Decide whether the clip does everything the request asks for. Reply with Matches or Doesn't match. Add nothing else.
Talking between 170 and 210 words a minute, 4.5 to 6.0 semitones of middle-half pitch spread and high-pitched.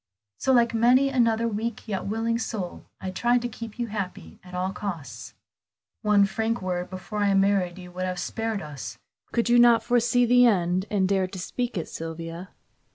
Doesn't match